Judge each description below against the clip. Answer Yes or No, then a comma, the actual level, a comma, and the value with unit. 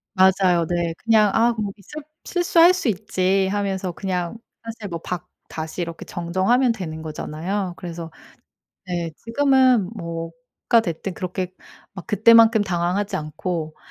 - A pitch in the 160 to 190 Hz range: Yes, medium, 185 Hz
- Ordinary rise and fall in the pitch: Yes, average, 4.4 semitones